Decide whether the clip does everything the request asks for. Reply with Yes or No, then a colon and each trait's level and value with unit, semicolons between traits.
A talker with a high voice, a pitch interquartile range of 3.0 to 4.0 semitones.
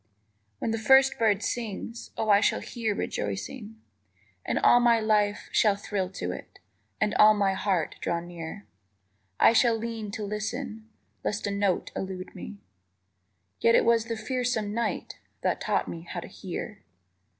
No: high, 210 Hz; narrow, 2.5 semitones